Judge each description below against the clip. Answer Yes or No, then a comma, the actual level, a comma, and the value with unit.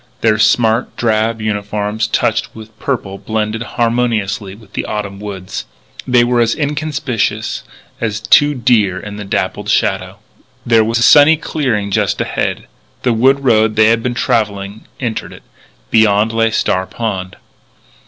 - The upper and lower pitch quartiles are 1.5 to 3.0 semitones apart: Yes, narrow, 2.5 semitones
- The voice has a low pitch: Yes, low, 110 Hz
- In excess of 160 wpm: No, average, 145 wpm